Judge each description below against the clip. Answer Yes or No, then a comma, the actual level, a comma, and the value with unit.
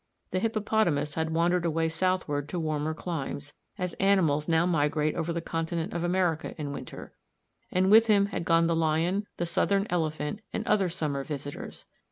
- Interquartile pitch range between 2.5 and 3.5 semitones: Yes, average, 3.0 semitones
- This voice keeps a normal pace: Yes, average, 170 wpm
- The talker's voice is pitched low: No, medium, 165 Hz